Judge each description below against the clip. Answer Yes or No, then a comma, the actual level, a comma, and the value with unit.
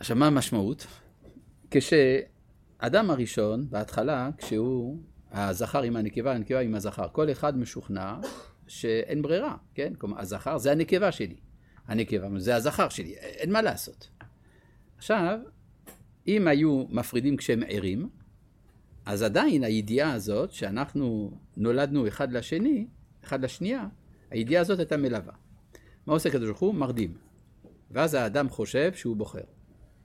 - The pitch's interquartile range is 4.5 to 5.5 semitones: Yes, average, 5.2 semitones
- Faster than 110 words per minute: Yes, average, 120 wpm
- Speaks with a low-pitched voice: Yes, low, 125 Hz